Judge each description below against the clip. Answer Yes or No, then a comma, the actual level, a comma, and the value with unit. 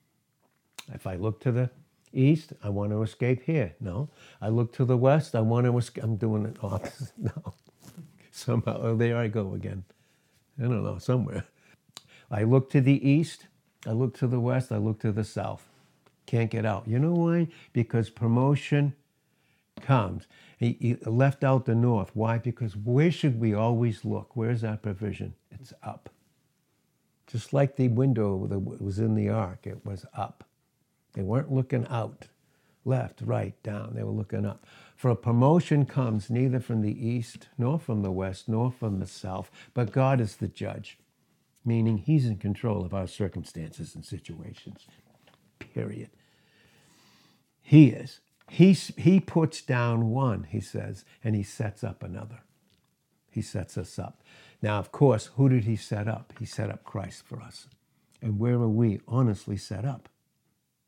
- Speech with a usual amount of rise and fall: Yes, average, 3.7 semitones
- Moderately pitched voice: No, low, 115 Hz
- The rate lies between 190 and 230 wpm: No, average, 170 wpm